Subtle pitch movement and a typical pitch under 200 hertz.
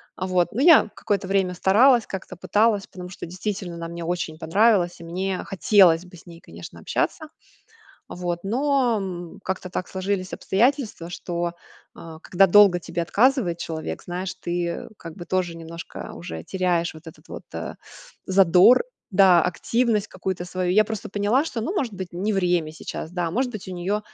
No: average, 3.0 semitones; medium, 185 Hz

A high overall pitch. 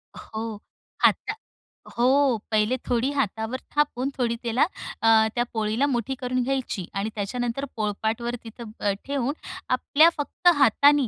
Yes: high, 240 Hz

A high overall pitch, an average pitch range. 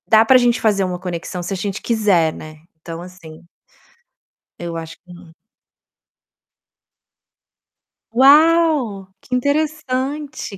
No: high, 205 Hz; wide, 7.0 semitones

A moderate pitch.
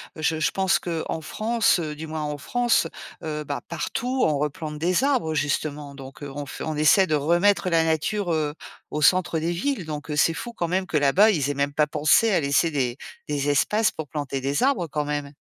Yes: medium, 155 Hz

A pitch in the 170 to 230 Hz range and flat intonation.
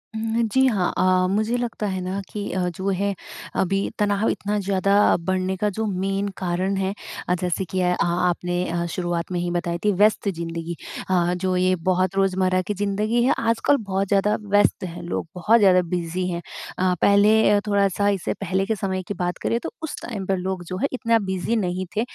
Yes: high, 190 Hz; narrow, 2.3 semitones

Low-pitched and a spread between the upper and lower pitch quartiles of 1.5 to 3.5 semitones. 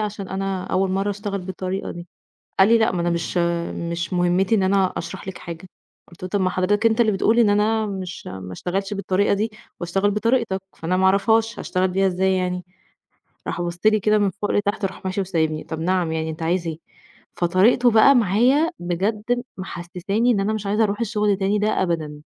No: high, 190 Hz; average, 2.8 semitones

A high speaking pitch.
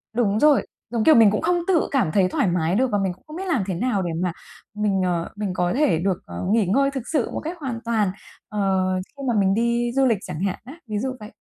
Yes: high, 210 Hz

